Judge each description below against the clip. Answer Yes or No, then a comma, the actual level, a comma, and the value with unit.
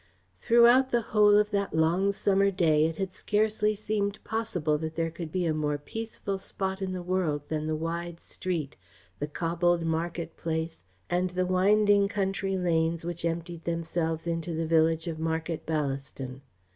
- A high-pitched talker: No, medium, 170 Hz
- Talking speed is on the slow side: No, average, 165 wpm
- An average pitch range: Yes, average, 3.3 semitones